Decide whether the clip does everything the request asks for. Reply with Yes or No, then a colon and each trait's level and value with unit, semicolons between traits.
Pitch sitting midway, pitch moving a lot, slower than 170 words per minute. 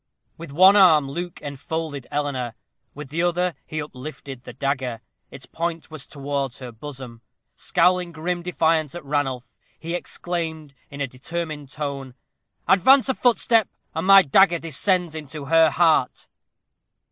No: medium, 155 Hz; average, 3.9 semitones; average, 140 wpm